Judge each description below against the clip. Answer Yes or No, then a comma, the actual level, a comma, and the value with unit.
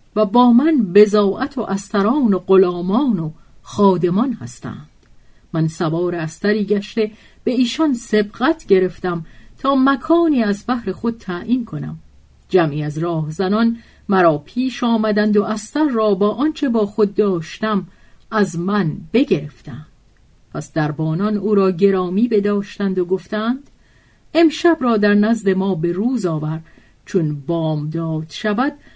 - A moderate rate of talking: Yes, average, 135 wpm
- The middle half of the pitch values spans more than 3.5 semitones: Yes, average, 5.1 semitones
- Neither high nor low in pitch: No, high, 205 Hz